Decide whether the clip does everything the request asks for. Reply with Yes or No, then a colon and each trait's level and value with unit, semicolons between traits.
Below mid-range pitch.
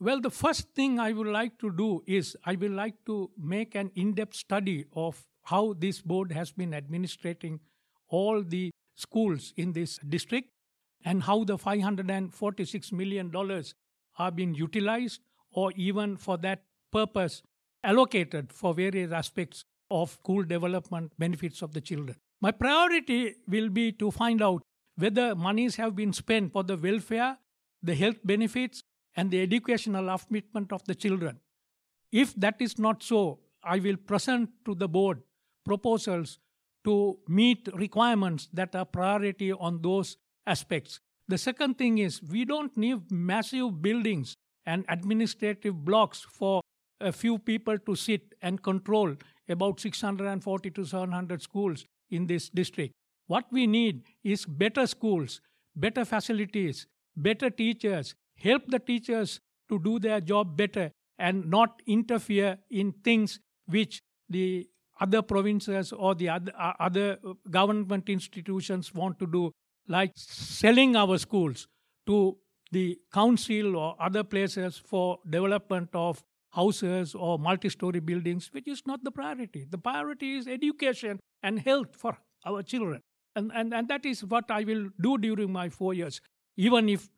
No: high, 195 Hz